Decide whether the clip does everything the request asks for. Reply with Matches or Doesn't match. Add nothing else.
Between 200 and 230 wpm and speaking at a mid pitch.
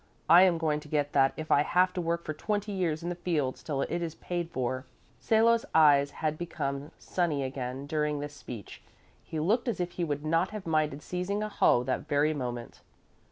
Matches